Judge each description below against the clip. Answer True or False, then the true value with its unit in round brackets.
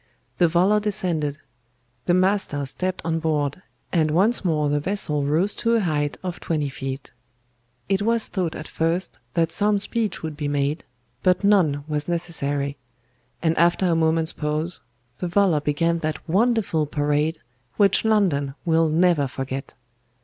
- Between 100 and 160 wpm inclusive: True (150 wpm)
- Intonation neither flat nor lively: True (4.0 semitones)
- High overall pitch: False (165 Hz)